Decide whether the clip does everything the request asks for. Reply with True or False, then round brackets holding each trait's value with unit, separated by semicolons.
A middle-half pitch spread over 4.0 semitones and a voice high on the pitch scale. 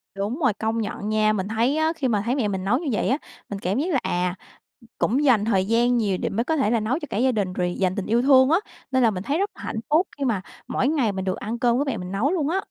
True (5.0 semitones; 230 Hz)